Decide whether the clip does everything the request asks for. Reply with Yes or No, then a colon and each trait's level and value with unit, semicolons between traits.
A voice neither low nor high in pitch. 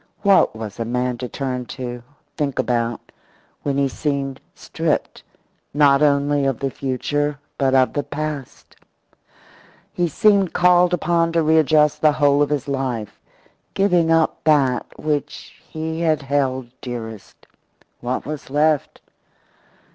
Yes: medium, 145 Hz